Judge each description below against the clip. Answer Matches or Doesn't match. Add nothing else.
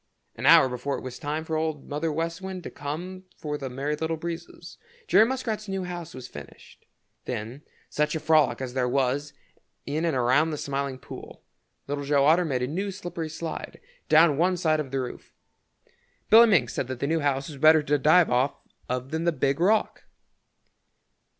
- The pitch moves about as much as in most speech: Matches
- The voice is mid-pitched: Matches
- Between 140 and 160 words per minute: Doesn't match